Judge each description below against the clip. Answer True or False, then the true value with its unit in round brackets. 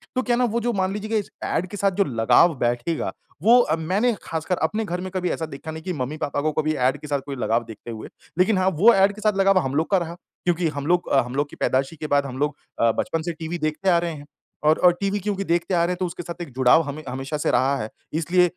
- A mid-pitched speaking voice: True (165 Hz)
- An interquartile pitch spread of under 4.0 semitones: False (4.8 semitones)